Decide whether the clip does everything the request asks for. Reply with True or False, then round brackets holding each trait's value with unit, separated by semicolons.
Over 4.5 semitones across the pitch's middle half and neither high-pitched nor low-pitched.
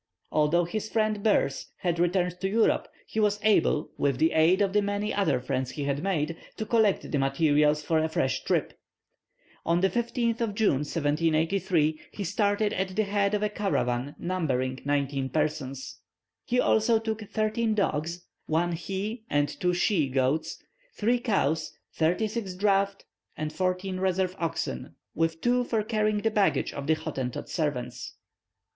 True (5.6 semitones; 180 Hz)